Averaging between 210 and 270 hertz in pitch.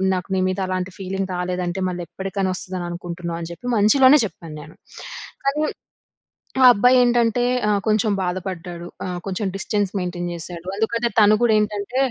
No: high, 190 Hz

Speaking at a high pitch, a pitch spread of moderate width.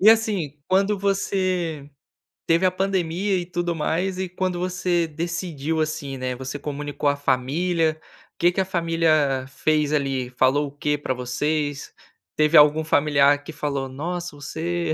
No: medium, 155 Hz; average, 3.7 semitones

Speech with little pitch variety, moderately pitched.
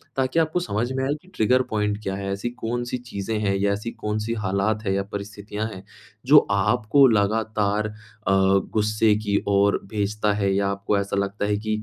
No: narrow, 2.0 semitones; low, 105 Hz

